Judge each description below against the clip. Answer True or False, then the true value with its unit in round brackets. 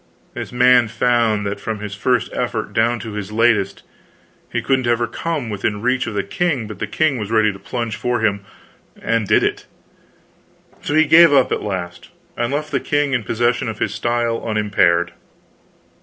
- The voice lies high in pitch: False (115 Hz)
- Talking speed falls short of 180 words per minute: False (185 wpm)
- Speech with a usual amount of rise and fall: True (3.0 semitones)